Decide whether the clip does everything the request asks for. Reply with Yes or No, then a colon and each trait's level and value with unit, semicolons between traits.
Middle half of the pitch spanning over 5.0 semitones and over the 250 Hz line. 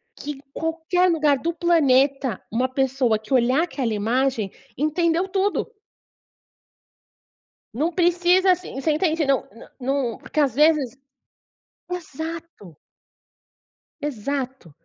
No: average, 4.5 semitones; very high, 285 Hz